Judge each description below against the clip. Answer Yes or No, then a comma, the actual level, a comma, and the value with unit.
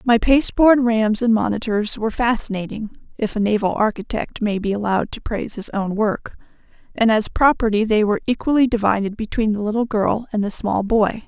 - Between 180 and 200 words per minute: No, average, 170 wpm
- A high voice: Yes, high, 220 Hz